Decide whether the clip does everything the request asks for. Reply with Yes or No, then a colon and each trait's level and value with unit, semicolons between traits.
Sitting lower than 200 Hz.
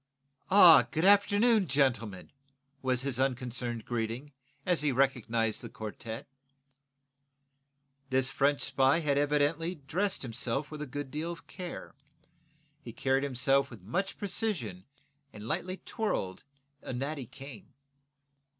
Yes: low, 135 Hz